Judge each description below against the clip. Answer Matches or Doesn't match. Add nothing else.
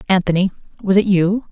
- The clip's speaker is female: Matches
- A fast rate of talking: Doesn't match